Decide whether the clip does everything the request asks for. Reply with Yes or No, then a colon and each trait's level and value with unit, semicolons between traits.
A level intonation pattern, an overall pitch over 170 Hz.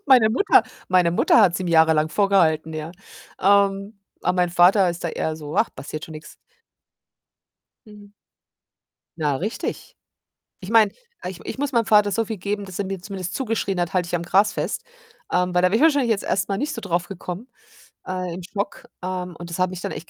No: average, 3.1 semitones; medium, 185 Hz